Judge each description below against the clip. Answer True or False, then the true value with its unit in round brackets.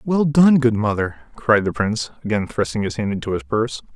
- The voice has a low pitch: True (110 Hz)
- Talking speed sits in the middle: False (210 wpm)